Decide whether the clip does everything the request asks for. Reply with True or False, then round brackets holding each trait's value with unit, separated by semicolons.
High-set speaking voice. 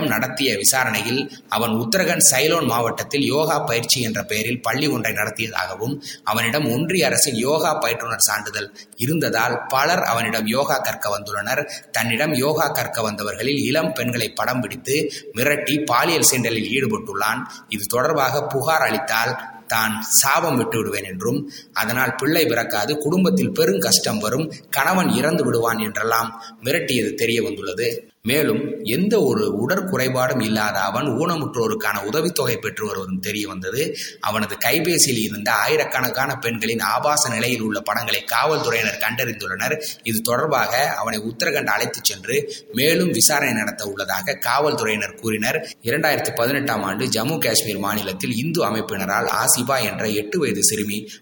False (120 Hz)